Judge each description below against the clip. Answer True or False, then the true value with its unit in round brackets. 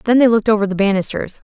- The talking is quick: True (240 wpm)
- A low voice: False (210 Hz)